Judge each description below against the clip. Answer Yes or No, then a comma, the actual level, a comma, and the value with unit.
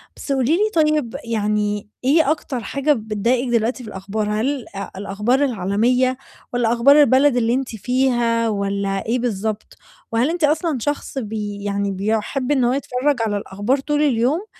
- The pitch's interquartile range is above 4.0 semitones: Yes, average, 4.4 semitones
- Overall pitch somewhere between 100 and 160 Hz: No, high, 240 Hz